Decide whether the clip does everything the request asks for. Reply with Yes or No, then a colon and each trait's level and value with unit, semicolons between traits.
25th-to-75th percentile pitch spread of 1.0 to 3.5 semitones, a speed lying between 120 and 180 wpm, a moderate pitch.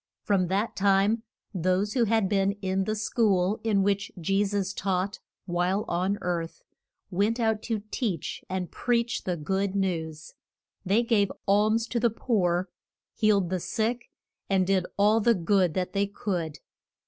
No: average, 2.8 semitones; average, 155 wpm; high, 195 Hz